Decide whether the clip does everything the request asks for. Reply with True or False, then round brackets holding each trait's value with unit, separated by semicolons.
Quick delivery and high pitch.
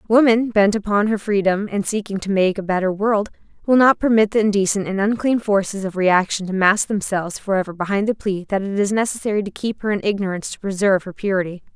True (215 wpm; 200 Hz)